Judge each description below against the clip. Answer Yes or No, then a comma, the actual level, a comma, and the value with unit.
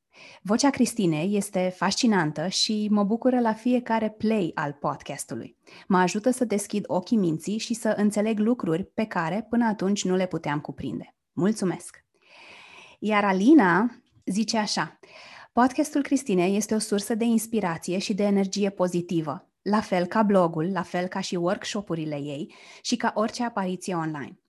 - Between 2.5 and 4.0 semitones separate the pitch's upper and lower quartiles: Yes, average, 3.7 semitones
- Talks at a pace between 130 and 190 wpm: Yes, average, 150 wpm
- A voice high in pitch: Yes, high, 205 Hz